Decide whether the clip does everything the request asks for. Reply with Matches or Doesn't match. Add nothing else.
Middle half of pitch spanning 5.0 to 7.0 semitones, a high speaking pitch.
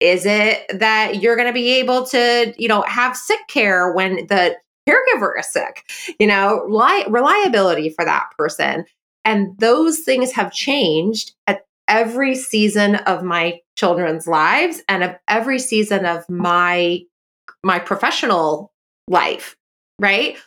Matches